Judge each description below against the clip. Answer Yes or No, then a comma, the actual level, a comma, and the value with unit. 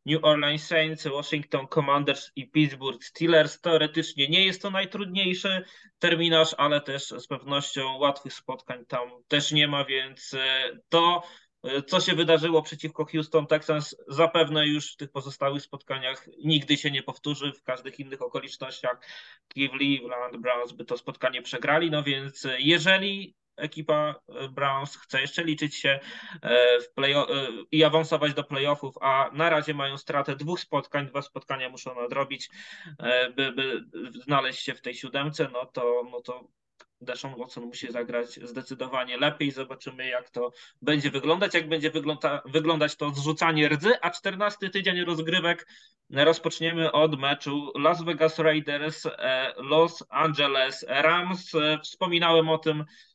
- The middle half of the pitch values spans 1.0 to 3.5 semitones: Yes, average, 2.9 semitones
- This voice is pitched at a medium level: Yes, medium, 145 Hz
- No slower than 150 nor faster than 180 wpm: No, average, 140 wpm